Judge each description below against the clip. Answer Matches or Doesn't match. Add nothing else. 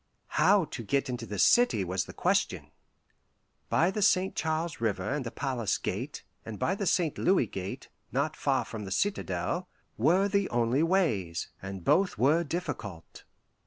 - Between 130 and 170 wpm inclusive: Matches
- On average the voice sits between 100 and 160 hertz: Matches